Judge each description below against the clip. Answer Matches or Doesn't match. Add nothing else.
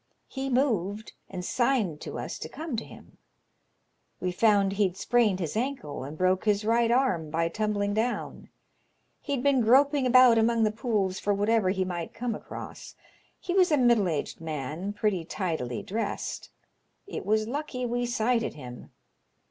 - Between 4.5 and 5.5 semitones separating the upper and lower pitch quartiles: Matches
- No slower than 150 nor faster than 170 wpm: Matches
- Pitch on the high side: Matches